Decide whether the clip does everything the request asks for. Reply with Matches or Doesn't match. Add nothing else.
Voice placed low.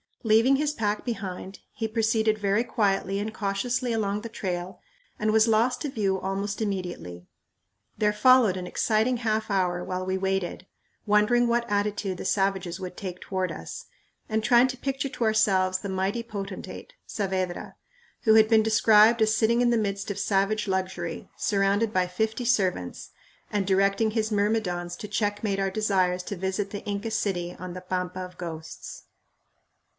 Doesn't match